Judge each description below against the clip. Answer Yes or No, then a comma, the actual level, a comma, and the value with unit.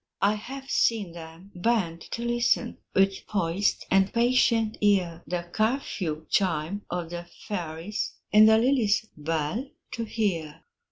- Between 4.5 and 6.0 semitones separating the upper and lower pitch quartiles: Yes, average, 5.0 semitones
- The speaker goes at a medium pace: No, slow, 130 wpm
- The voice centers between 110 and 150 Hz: No, high, 200 Hz